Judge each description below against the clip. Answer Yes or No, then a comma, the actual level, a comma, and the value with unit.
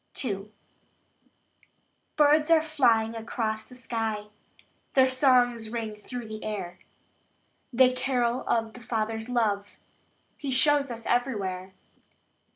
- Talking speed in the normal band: No, slow, 110 wpm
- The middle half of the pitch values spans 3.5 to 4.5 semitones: No, average, 2.8 semitones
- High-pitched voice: Yes, high, 235 Hz